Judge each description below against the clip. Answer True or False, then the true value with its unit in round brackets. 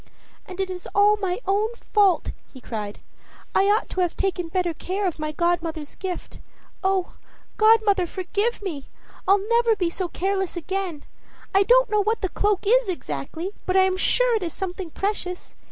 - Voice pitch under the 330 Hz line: False (380 Hz)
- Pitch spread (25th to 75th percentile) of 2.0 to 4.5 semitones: True (2.8 semitones)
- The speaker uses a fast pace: False (175 wpm)